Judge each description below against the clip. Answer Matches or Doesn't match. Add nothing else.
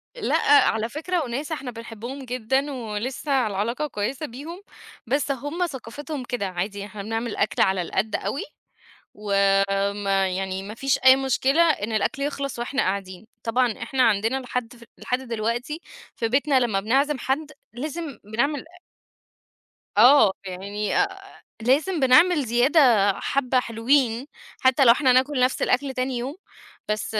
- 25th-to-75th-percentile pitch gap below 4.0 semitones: Doesn't match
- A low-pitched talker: Doesn't match